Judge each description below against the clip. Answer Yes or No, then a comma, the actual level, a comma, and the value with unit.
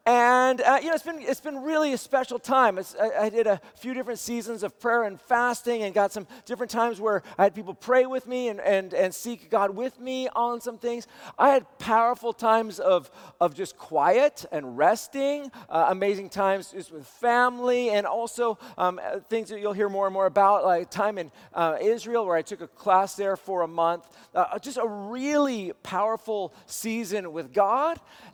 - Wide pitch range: No, average, 4.0 semitones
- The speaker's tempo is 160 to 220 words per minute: Yes, average, 200 wpm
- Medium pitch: No, high, 225 Hz